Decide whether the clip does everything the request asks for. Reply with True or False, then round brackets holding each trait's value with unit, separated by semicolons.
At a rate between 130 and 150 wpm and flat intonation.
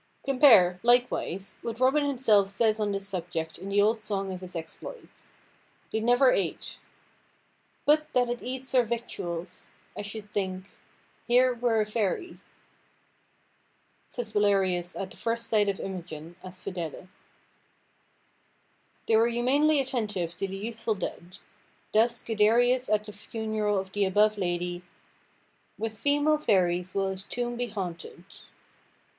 False (140 wpm; 4.2 semitones)